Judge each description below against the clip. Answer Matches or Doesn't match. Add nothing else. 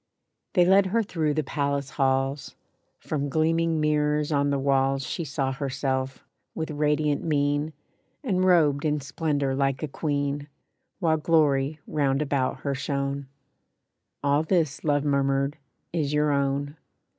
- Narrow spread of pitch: Matches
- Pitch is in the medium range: Matches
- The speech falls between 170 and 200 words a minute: Doesn't match